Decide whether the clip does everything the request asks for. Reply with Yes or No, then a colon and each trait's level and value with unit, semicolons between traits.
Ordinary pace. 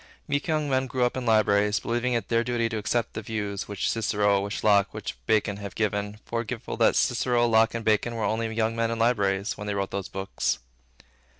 No: fast, 210 wpm